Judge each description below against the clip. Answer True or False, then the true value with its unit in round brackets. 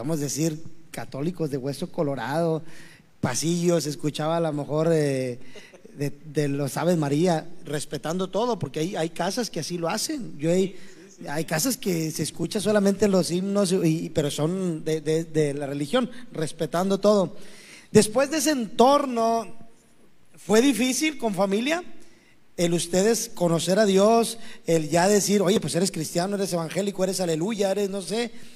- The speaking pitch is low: False (175 Hz)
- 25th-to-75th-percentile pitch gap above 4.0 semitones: True (4.6 semitones)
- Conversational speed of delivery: True (160 wpm)